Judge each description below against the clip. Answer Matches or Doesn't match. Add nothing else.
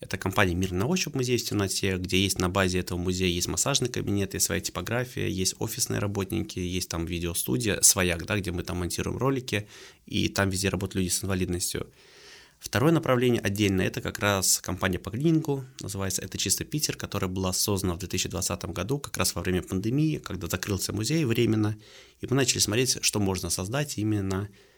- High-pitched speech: Doesn't match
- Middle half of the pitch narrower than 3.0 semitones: Doesn't match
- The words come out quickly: Matches